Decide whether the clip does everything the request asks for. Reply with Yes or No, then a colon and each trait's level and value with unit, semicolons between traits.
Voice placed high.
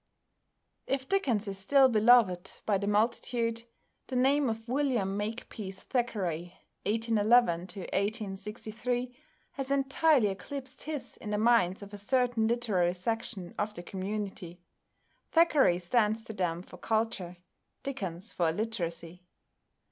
Yes: high, 215 Hz